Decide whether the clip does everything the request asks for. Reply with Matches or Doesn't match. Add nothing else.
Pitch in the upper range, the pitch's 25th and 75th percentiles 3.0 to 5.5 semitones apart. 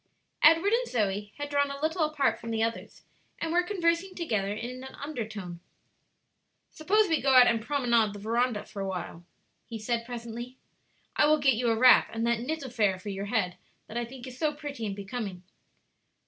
Matches